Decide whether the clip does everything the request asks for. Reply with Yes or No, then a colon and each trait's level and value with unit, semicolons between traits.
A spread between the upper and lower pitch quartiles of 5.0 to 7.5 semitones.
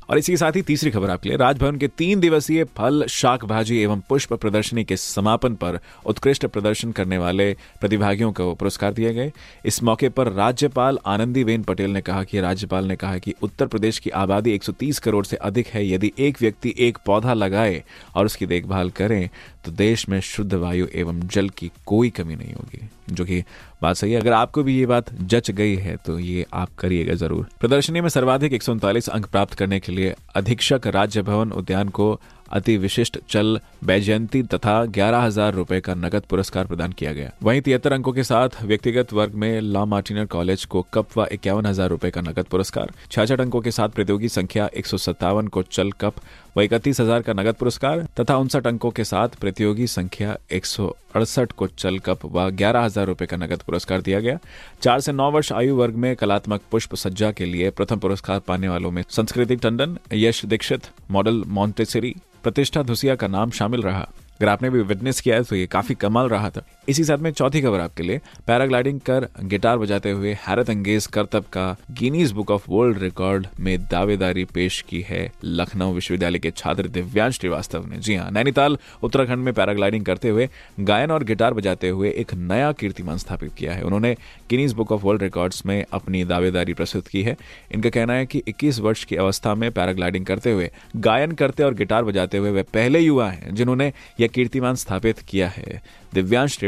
No: average, 4.1 semitones